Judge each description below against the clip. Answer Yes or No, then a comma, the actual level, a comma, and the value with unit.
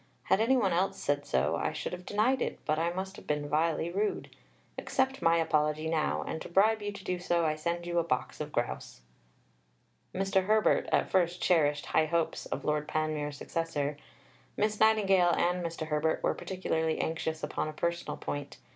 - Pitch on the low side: No, medium, 170 Hz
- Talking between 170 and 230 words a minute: Yes, average, 190 wpm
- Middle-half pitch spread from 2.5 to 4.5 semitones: Yes, average, 3.7 semitones